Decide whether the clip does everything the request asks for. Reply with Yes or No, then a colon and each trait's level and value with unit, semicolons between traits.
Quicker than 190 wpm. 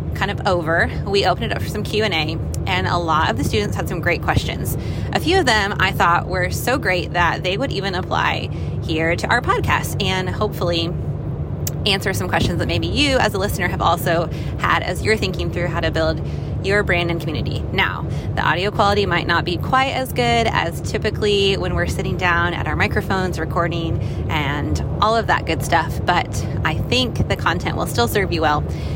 Yes: fast, 205 wpm